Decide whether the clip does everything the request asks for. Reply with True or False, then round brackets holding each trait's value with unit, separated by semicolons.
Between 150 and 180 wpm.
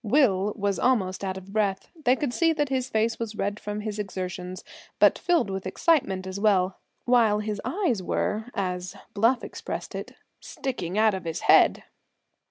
True (175 wpm)